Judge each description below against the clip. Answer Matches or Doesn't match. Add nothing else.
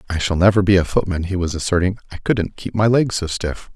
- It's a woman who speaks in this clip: Doesn't match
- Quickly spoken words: Matches